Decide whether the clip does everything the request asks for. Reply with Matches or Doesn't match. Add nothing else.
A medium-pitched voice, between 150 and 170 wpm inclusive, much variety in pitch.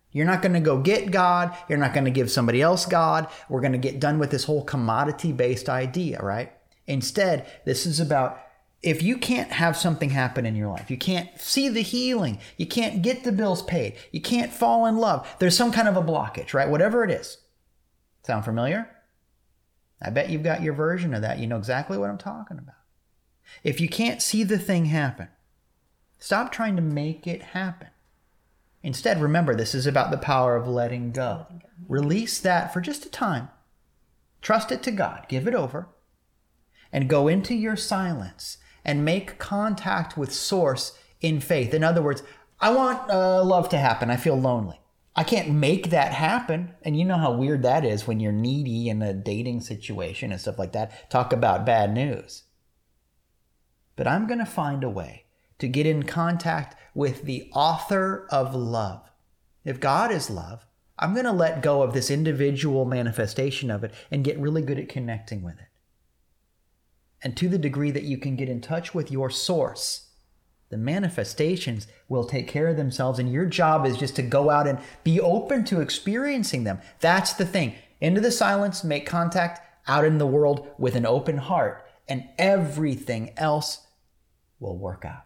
Doesn't match